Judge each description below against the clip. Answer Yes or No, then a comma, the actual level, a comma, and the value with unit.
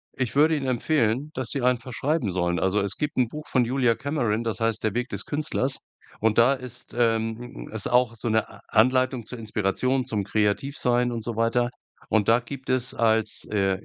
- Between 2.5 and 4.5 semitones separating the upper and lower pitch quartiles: Yes, average, 2.8 semitones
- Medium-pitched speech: No, low, 120 Hz